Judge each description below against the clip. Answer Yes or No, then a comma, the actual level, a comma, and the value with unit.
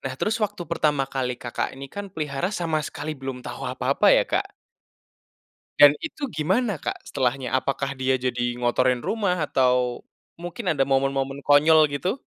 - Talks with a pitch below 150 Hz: Yes, medium, 140 Hz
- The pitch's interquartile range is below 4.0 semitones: No, average, 4.6 semitones